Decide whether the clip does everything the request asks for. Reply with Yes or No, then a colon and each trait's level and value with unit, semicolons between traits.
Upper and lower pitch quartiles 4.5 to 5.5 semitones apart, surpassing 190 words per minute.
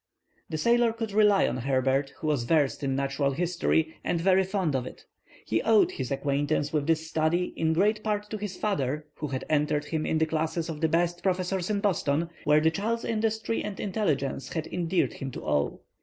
Yes: average, 5.1 semitones; average, 200 wpm